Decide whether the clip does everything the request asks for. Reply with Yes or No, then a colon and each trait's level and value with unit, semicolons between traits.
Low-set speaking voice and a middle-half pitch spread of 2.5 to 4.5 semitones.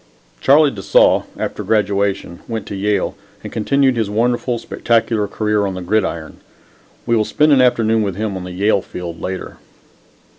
Yes: low, 105 Hz; average, 3.2 semitones